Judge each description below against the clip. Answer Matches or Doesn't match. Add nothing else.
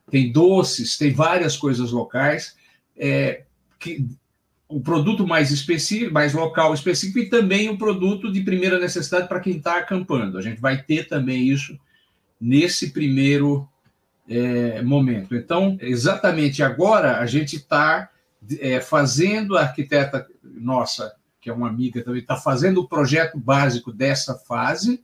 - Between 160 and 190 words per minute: Doesn't match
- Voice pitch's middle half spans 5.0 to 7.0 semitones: Matches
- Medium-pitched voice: Matches